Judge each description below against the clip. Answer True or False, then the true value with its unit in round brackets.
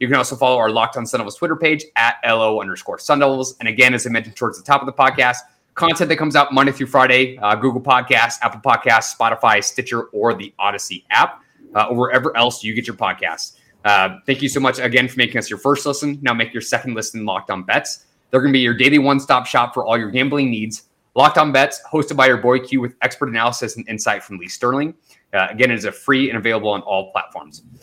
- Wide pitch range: False (3.3 semitones)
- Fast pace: True (240 wpm)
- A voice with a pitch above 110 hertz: True (125 Hz)